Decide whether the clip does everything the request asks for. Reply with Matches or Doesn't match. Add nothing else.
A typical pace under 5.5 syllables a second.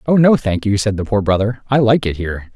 Doesn't match